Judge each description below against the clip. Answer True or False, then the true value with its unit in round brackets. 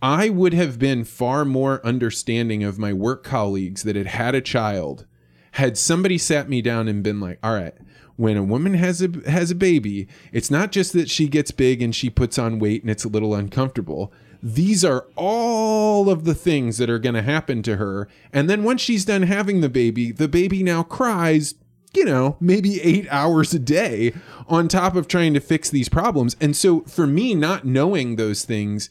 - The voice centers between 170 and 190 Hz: False (135 Hz)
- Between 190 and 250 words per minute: True (205 wpm)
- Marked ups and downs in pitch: True (7.3 semitones)